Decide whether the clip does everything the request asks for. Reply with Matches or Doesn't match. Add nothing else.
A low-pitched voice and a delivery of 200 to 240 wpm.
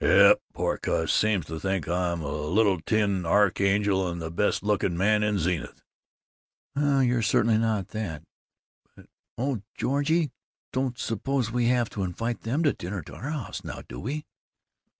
Doesn't match